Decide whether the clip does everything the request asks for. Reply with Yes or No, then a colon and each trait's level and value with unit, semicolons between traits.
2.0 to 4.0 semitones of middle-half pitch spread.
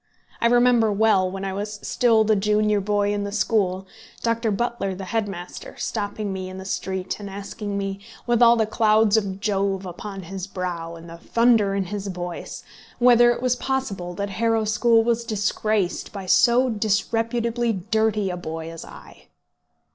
Yes: average, 2.9 semitones